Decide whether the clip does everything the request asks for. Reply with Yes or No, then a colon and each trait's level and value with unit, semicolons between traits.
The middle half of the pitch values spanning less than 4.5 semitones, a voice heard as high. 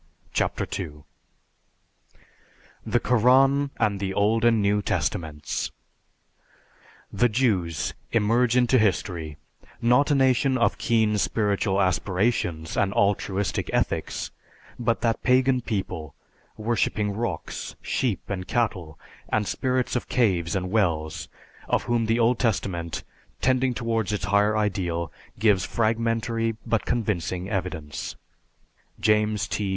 No: average, 4.0 semitones; low, 105 Hz